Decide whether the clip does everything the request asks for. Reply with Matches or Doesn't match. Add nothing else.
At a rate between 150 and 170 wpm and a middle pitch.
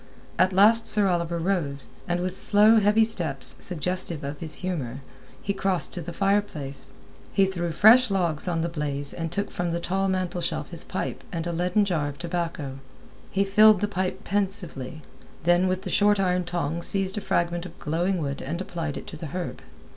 Doesn't match